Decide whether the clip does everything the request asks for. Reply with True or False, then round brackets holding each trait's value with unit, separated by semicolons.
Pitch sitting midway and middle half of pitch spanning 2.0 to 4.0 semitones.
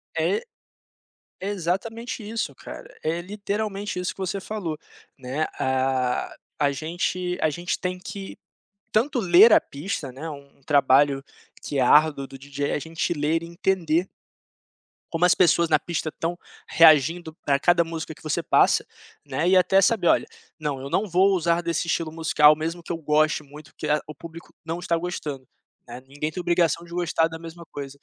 True (165 Hz; 3.3 semitones)